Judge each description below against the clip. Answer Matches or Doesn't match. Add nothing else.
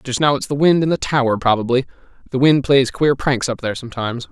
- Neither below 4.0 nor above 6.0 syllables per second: Doesn't match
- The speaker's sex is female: Doesn't match